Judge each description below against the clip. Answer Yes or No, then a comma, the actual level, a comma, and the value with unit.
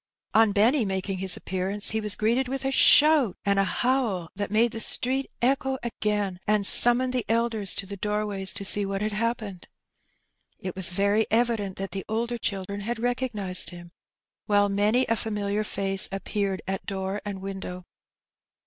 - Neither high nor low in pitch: No, high, 205 Hz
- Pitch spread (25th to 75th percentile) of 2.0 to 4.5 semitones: Yes, average, 3.1 semitones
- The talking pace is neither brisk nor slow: Yes, average, 175 wpm